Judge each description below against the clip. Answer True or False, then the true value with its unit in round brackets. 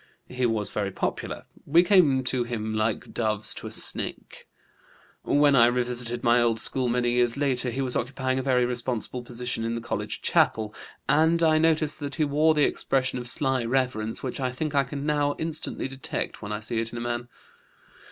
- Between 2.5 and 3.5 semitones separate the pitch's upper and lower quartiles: True (3.1 semitones)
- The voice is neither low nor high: False (125 Hz)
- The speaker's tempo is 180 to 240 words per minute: True (195 wpm)